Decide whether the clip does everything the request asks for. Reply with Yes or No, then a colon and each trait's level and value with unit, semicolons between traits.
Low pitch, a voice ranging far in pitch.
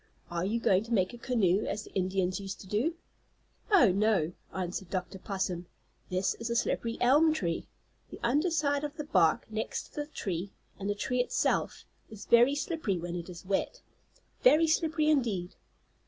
No: high, 210 Hz; wide, 7.1 semitones